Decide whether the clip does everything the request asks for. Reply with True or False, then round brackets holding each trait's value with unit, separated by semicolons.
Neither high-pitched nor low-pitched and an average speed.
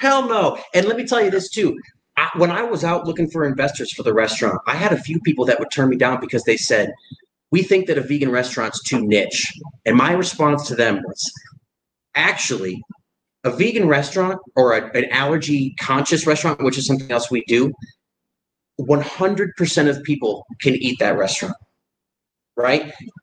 True (150 Hz; 185 wpm)